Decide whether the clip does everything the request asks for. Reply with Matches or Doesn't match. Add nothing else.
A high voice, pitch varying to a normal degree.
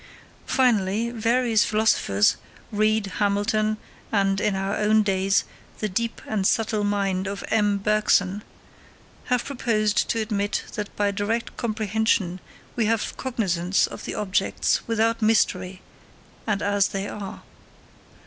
Doesn't match